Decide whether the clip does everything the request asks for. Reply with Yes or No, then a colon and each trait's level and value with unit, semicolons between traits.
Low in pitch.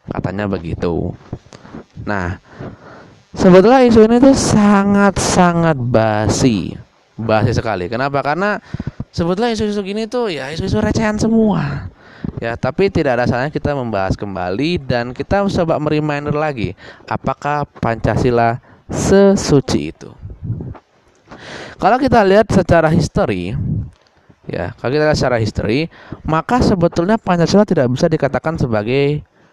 No: medium, 150 Hz